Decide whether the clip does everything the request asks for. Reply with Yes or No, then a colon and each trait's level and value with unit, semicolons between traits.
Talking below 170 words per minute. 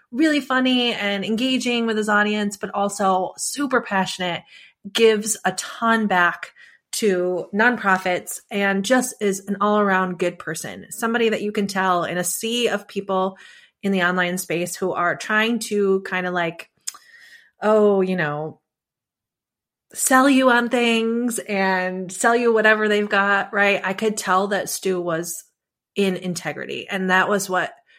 Yes: average, 155 wpm